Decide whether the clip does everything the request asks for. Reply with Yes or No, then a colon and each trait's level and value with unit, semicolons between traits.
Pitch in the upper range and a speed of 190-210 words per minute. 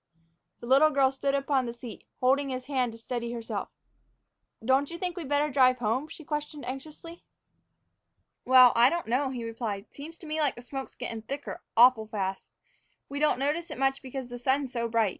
Yes: very high, 265 Hz; average, 195 wpm